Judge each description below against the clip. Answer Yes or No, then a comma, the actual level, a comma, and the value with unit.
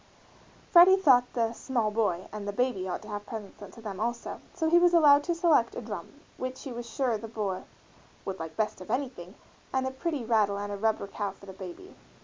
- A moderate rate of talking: No, fast, 225 wpm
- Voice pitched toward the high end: Yes, high, 230 Hz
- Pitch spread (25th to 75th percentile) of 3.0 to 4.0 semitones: No, average, 4.6 semitones